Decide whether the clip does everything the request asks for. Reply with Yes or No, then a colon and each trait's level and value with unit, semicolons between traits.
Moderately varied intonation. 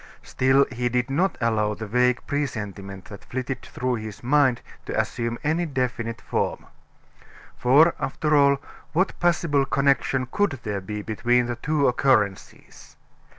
Yes: average, 3.4 semitones